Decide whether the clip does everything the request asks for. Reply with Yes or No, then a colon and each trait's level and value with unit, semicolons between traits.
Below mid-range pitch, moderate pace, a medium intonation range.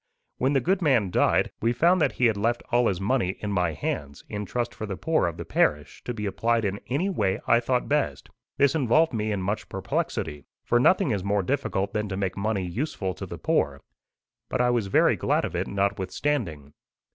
No: low, 110 Hz; fast, 215 wpm; average, 4.7 semitones